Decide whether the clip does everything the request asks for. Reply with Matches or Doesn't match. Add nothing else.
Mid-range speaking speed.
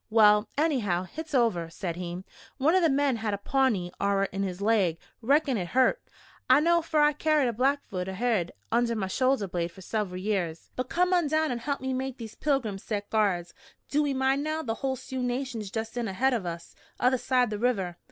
Doesn't match